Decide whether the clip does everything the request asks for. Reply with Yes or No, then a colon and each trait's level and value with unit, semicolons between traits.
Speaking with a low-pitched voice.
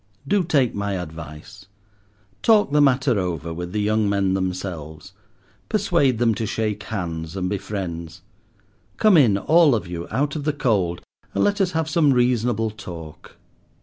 Yes: low, 105 Hz